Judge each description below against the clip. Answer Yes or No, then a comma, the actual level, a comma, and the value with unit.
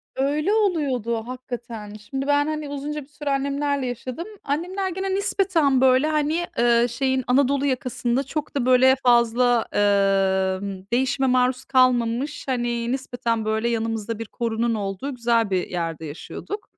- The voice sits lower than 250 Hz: No, very high, 255 Hz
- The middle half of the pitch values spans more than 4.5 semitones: No, average, 3.7 semitones